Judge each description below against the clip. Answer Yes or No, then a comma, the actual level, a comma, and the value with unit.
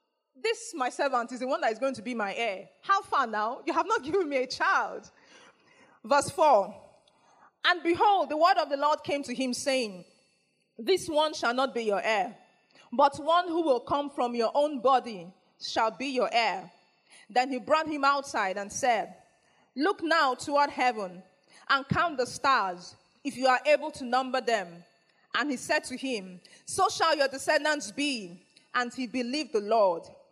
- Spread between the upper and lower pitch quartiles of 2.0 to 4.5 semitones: Yes, average, 4.2 semitones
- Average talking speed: Yes, average, 185 wpm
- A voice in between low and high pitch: No, very high, 270 Hz